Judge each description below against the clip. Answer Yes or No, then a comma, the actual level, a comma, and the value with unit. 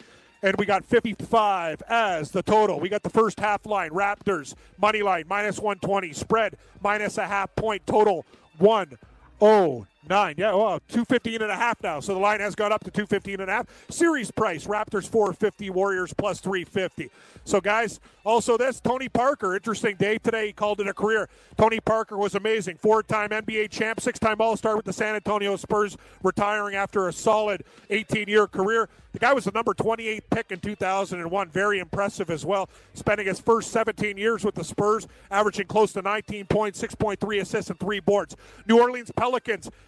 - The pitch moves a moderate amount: No, narrow, 1.9 semitones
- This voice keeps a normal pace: Yes, average, 180 wpm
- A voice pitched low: No, high, 210 Hz